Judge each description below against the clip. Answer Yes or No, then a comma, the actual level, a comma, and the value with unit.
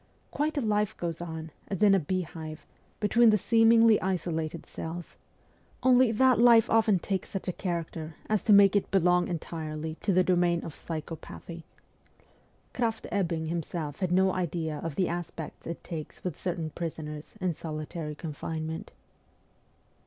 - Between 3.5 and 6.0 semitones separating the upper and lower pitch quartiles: Yes, average, 3.9 semitones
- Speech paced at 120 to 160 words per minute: Yes, average, 155 wpm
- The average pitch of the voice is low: No, medium, 175 Hz